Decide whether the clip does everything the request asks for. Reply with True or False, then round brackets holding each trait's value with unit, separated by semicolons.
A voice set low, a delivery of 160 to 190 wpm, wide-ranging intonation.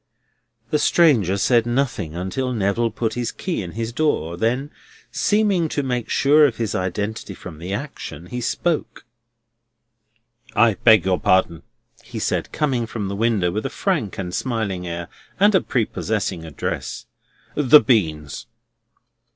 False (115 Hz; 145 wpm; 6.3 semitones)